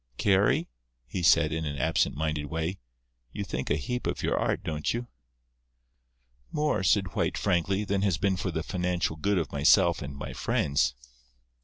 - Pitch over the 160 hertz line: No, very low, 85 Hz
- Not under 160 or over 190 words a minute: Yes, average, 170 wpm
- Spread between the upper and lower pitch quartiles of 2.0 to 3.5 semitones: No, average, 4.2 semitones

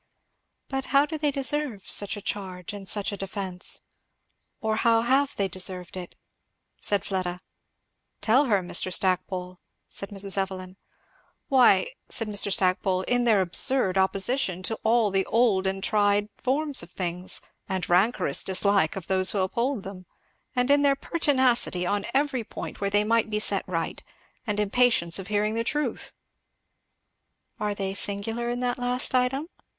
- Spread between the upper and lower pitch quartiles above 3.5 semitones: Yes, average, 4.6 semitones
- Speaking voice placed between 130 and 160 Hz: No, high, 205 Hz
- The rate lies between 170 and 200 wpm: No, average, 155 wpm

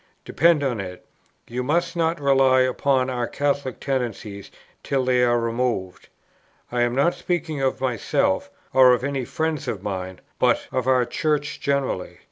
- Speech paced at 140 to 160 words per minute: Yes, average, 155 wpm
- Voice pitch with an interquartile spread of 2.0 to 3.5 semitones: Yes, average, 3.0 semitones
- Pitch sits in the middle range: No, low, 130 Hz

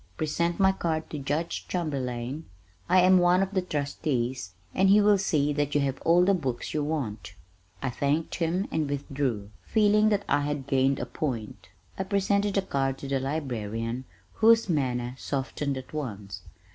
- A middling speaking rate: Yes, average, 170 wpm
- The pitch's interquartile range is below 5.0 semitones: No, wide, 5.5 semitones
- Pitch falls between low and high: Yes, medium, 145 Hz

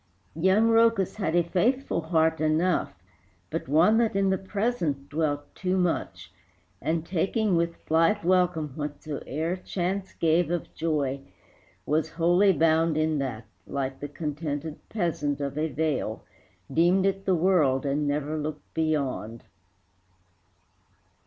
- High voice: No, medium, 160 Hz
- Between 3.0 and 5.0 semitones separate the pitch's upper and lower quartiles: Yes, average, 3.8 semitones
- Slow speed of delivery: Yes, slow, 130 wpm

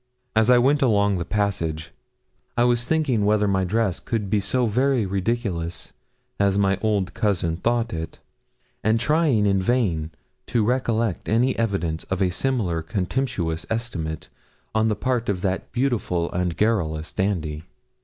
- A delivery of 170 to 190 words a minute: No, average, 150 wpm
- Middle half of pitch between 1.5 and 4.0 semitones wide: No, average, 4.7 semitones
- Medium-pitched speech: No, low, 105 Hz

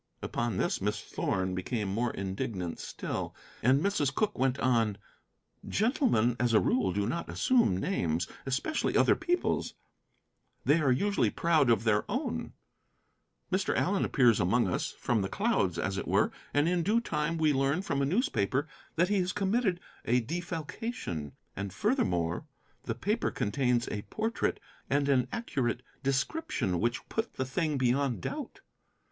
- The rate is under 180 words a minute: Yes, average, 150 wpm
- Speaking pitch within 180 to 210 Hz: No, low, 135 Hz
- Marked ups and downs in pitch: Yes, wide, 8.9 semitones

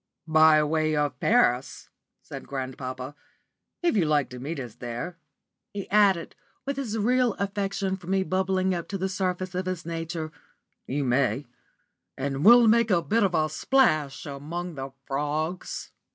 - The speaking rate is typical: Yes, average, 155 wpm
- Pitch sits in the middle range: Yes, medium, 170 Hz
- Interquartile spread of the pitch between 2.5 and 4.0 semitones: No, average, 5.2 semitones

